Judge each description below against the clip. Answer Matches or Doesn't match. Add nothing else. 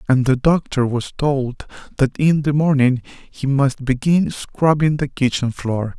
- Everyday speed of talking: Matches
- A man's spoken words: Matches